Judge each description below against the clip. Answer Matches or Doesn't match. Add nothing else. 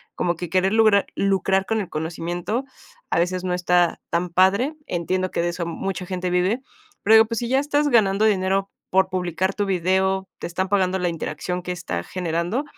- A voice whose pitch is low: Doesn't match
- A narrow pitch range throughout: Matches